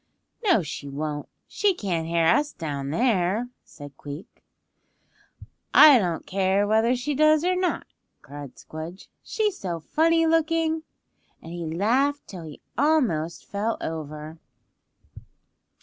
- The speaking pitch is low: No, high, 195 Hz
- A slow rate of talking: Yes, slow, 125 wpm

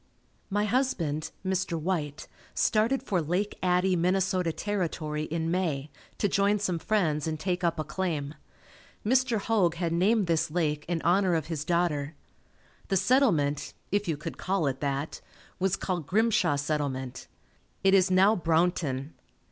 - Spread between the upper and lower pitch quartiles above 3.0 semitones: Yes, average, 4.0 semitones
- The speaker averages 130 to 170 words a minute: Yes, average, 150 wpm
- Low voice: No, medium, 175 Hz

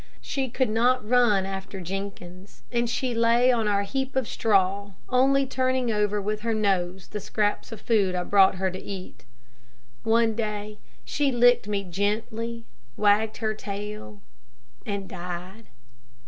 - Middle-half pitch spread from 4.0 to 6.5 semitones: No, average, 3.2 semitones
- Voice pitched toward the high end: Yes, high, 210 Hz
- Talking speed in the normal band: Yes, average, 145 wpm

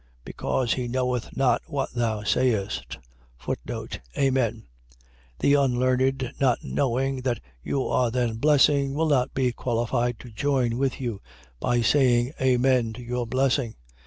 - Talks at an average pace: No, slow, 130 wpm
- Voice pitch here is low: Yes, low, 125 Hz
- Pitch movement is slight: Yes, narrow, 2.0 semitones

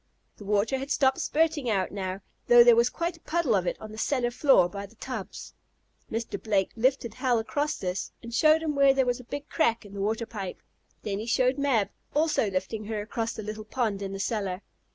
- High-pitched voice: Yes, high, 230 Hz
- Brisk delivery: Yes, fast, 220 wpm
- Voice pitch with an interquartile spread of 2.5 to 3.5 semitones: No, average, 4.6 semitones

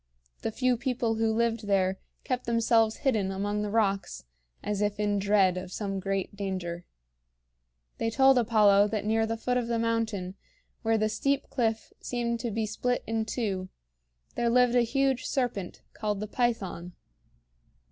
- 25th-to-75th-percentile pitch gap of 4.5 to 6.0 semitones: No, average, 2.7 semitones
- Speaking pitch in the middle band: No, high, 220 Hz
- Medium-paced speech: Yes, average, 160 wpm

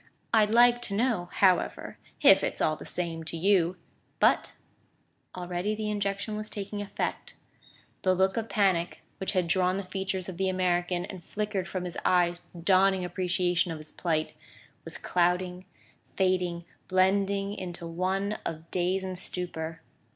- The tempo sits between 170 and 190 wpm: No, average, 160 wpm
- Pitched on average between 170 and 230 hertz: Yes, medium, 185 Hz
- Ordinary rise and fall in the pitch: No, narrow, 2.0 semitones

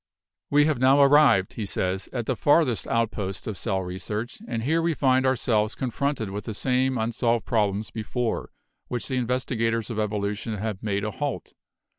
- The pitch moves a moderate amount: Yes, average, 3.8 semitones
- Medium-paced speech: Yes, average, 170 wpm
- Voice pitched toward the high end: No, low, 115 Hz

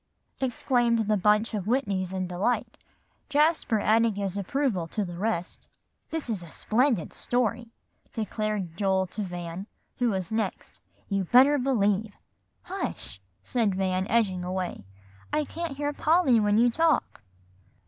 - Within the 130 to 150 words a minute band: Yes, average, 140 wpm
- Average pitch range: Yes, average, 4.6 semitones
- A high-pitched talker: Yes, high, 215 Hz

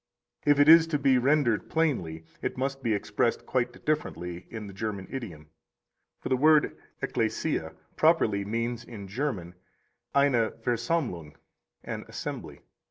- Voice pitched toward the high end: No, low, 120 Hz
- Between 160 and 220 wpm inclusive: No, slow, 135 wpm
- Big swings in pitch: Yes, wide, 6.0 semitones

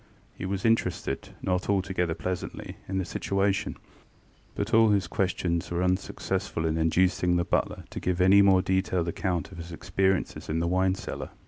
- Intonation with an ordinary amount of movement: No, narrow, 1.9 semitones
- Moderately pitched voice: No, very low, 95 Hz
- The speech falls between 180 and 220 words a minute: No, average, 165 wpm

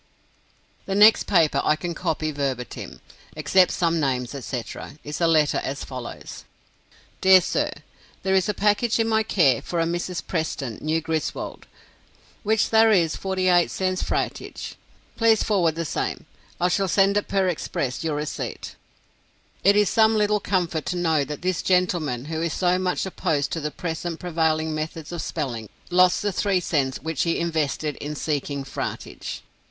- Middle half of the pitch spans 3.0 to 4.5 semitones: Yes, average, 3.8 semitones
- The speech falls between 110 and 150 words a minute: No, average, 165 wpm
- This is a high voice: No, medium, 170 Hz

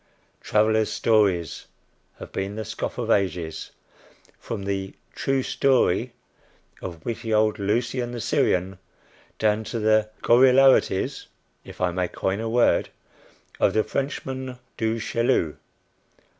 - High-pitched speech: No, low, 110 Hz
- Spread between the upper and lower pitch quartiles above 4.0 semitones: No, average, 3.7 semitones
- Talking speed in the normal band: No, slow, 120 wpm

